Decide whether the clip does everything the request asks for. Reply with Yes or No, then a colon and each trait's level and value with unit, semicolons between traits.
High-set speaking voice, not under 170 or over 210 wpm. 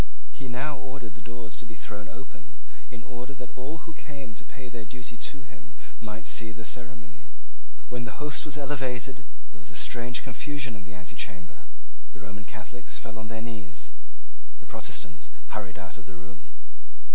No: low, 115 Hz; average, 180 wpm